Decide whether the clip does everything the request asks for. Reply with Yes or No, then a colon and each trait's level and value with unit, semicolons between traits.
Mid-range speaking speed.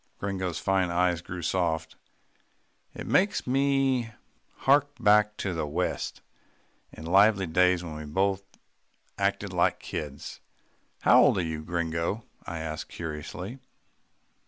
No: slow, 125 wpm